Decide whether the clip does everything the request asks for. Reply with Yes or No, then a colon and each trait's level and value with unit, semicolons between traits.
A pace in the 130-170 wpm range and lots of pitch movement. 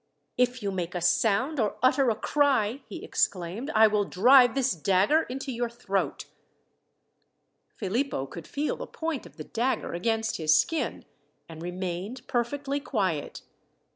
Yes: average, 145 wpm; wide, 5.9 semitones